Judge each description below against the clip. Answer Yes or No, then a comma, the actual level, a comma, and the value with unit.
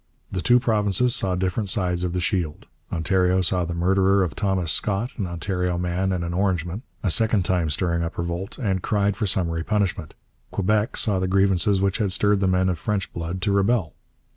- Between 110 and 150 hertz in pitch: No, very low, 95 Hz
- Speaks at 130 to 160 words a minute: No, average, 195 wpm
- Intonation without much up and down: Yes, narrow, 2.3 semitones